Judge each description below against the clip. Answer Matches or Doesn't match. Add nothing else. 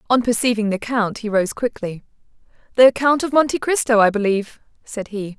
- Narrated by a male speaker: Doesn't match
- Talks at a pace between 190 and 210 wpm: Doesn't match